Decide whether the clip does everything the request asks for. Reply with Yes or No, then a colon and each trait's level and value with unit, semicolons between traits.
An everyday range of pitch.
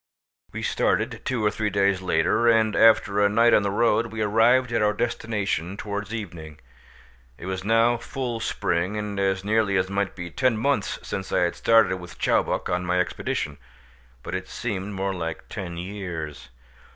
Yes: average, 3.3 semitones